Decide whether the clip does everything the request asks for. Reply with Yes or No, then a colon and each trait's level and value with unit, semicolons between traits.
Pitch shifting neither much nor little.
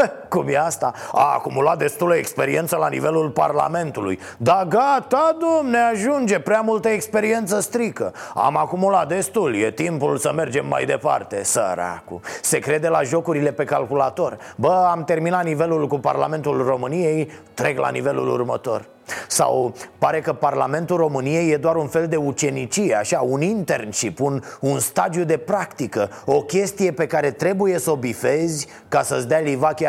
Yes: average, 4.5 semitones